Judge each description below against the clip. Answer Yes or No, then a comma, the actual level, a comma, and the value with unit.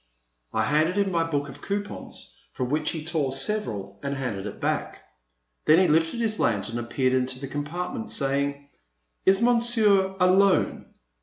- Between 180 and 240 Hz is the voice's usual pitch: No, medium, 150 Hz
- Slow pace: No, average, 165 wpm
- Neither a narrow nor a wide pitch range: No, wide, 6.5 semitones